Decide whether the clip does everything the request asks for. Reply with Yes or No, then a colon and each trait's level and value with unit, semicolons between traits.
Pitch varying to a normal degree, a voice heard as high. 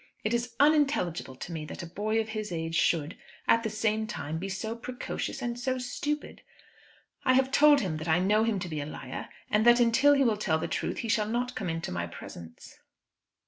No: wide, 6.5 semitones; high, 215 Hz